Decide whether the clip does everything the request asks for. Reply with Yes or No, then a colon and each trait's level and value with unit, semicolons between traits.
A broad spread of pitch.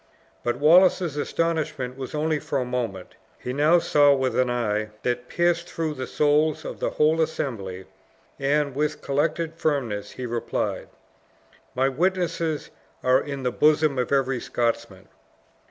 No: average, 3.8 semitones